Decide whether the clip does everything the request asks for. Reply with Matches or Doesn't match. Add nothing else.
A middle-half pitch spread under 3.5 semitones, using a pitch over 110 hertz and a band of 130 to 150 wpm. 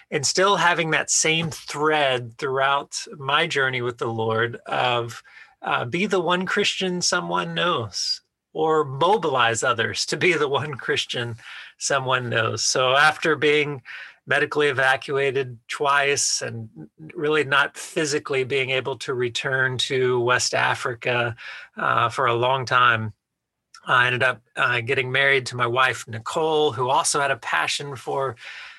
Doesn't match